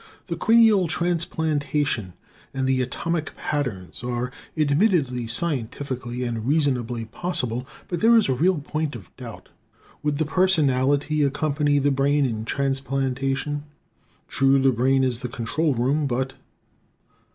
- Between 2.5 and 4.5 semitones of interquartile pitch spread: Yes, average, 3.4 semitones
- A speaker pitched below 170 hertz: Yes, low, 135 Hz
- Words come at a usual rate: No, slow, 130 wpm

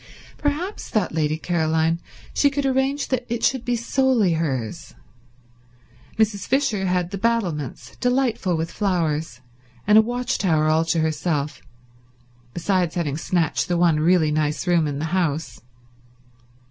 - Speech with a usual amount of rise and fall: No, wide, 6.7 semitones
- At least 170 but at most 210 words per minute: No, average, 140 wpm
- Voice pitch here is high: No, medium, 175 Hz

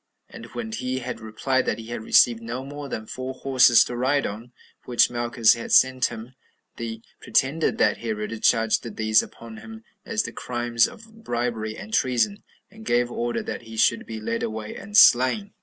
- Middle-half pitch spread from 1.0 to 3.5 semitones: Yes, average, 2.7 semitones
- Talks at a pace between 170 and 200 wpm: Yes, average, 185 wpm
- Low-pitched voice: Yes, low, 120 Hz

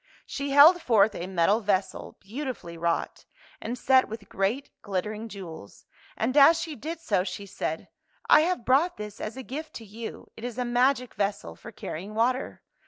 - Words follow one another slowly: No, average, 185 wpm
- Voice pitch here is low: No, high, 225 Hz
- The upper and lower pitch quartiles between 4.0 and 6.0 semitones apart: Yes, average, 5.2 semitones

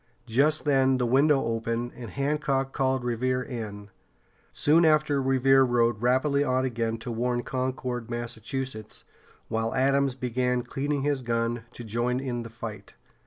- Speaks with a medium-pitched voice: No, low, 125 Hz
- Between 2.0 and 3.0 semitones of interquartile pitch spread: Yes, narrow, 2.5 semitones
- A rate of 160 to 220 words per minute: No, average, 145 wpm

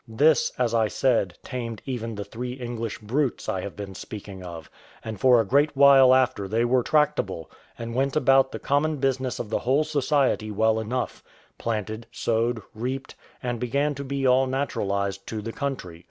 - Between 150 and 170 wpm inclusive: No, average, 180 wpm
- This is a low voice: Yes, low, 120 Hz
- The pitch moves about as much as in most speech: Yes, average, 3.7 semitones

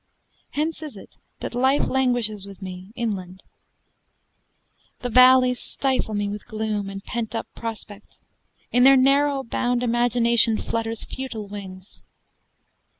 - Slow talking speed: Yes, slow, 125 wpm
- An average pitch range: Yes, average, 3.6 semitones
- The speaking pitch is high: Yes, high, 230 Hz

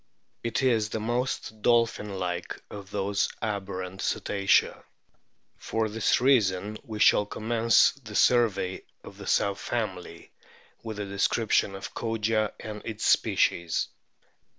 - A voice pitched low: Yes, low, 105 Hz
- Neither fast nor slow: No, slow, 125 wpm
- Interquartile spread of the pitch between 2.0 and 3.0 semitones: Yes, narrow, 2.5 semitones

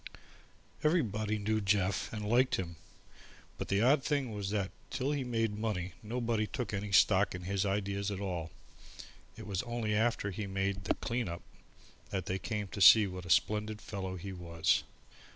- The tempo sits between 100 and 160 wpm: No, average, 175 wpm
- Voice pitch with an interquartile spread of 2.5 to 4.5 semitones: Yes, average, 2.8 semitones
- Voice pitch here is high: No, low, 105 Hz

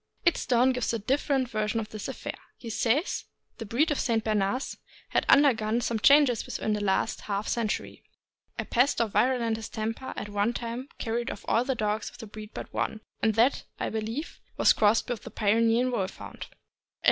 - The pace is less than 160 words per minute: No, average, 185 wpm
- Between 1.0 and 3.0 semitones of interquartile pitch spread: Yes, narrow, 2.6 semitones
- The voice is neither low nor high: No, high, 230 Hz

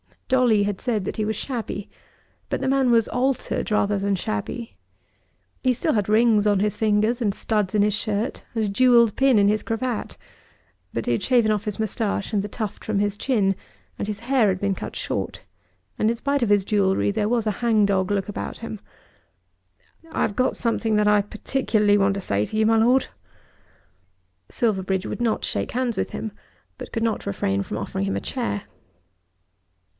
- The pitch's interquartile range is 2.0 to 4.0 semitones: Yes, narrow, 2.6 semitones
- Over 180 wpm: Yes, average, 195 wpm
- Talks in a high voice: Yes, high, 215 Hz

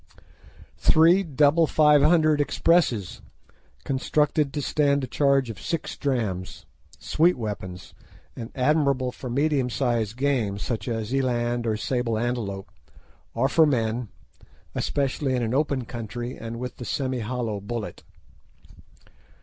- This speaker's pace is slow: Yes, slow, 125 wpm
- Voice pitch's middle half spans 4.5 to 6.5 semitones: No, average, 3.9 semitones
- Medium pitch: No, low, 125 Hz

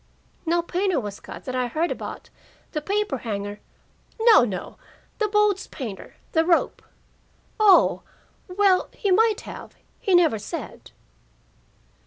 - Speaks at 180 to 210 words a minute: No, slow, 135 wpm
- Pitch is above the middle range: Yes, very high, 345 Hz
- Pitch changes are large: Yes, wide, 8.3 semitones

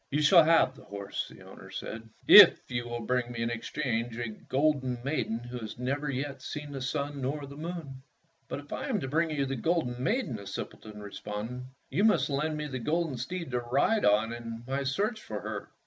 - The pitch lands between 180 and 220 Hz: No, low, 135 Hz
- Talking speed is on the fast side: Yes, fast, 215 wpm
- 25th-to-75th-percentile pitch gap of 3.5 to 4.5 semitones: Yes, average, 4.2 semitones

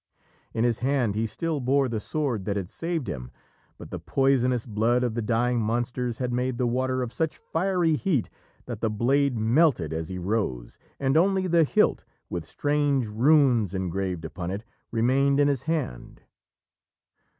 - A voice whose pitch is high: No, low, 125 Hz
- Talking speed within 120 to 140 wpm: No, average, 170 wpm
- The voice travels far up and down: No, average, 4.8 semitones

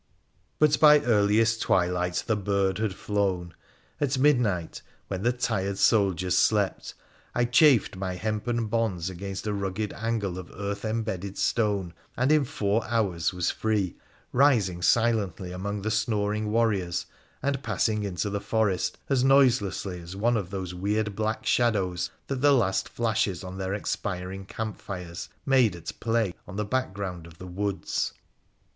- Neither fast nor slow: Yes, average, 150 wpm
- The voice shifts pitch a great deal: No, average, 3.5 semitones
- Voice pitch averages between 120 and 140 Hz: No, low, 100 Hz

